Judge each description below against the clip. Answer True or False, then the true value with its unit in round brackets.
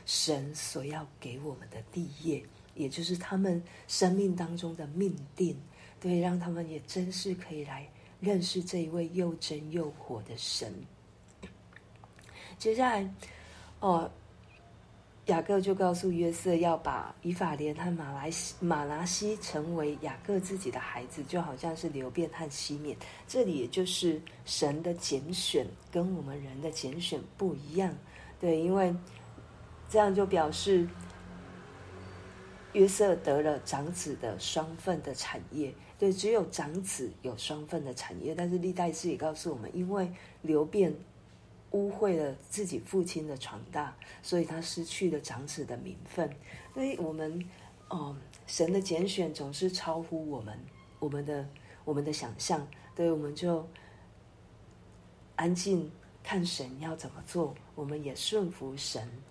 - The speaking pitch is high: False (160 Hz)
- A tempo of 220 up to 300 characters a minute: False (210 characters per minute)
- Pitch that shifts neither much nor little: True (4.1 semitones)